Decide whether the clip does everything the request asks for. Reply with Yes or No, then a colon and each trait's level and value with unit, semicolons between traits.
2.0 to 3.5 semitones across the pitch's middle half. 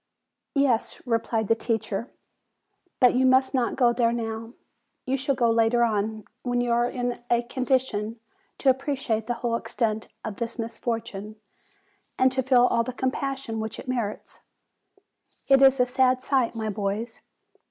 Yes: narrow, 2.4 semitones